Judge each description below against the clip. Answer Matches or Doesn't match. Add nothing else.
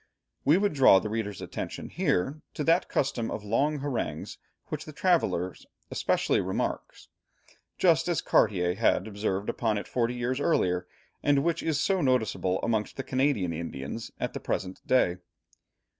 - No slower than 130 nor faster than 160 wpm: Matches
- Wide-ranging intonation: Matches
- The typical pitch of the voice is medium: Doesn't match